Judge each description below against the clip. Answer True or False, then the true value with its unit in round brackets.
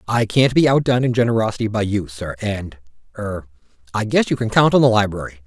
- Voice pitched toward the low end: True (110 Hz)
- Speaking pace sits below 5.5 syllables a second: False (6.1 syllables/s)